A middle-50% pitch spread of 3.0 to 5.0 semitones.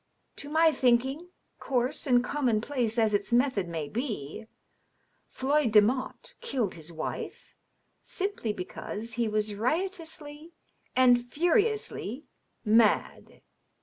No: wide, 5.6 semitones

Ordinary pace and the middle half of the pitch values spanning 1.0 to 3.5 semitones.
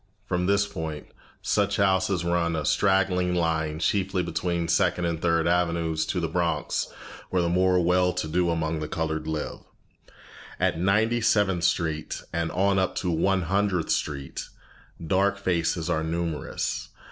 Yes: average, 150 wpm; narrow, 2.5 semitones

